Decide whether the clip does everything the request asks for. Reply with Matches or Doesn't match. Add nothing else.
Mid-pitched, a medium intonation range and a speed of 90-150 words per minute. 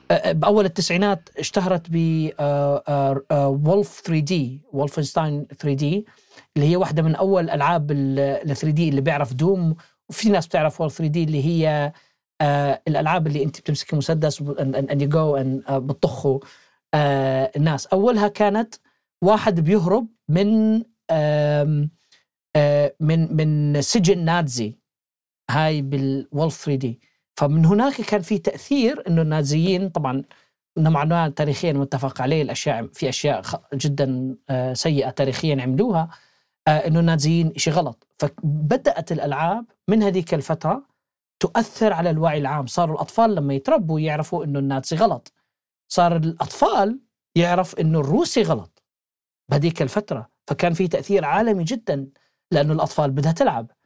Matches